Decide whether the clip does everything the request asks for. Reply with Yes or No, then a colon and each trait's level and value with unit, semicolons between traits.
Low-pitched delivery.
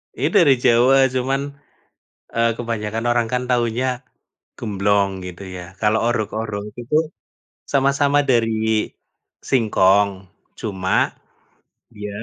Yes: low, 115 Hz